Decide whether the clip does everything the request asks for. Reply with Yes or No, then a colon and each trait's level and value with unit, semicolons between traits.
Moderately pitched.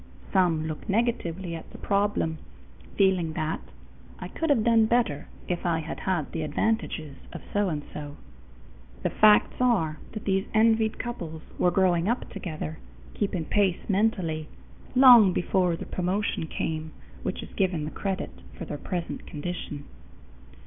Yes: medium, 180 Hz